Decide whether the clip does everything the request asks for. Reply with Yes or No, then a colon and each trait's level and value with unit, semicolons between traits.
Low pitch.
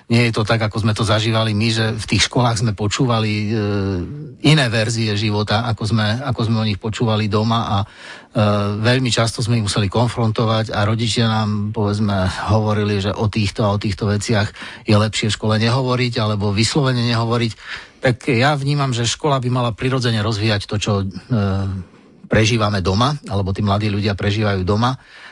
Yes: low, 110 Hz